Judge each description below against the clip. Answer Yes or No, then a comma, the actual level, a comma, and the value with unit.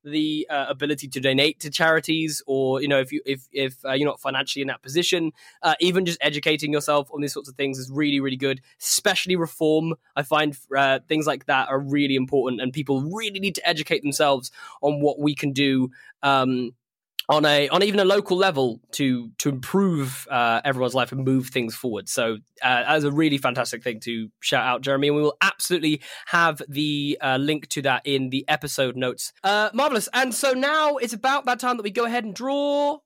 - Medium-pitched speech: Yes, medium, 145 Hz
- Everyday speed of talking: No, fast, 210 wpm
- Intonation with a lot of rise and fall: No, average, 3.9 semitones